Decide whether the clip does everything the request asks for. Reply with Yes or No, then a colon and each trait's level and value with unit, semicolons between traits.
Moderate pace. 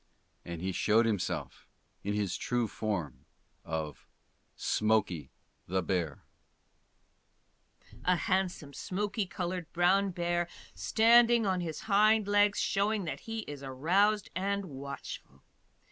No: slow, 115 wpm